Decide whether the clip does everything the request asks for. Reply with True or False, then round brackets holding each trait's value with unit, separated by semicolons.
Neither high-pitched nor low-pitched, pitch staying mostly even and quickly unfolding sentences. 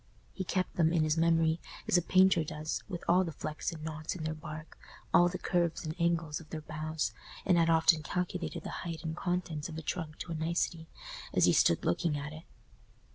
True (165 Hz; 1.8 semitones; 215 wpm)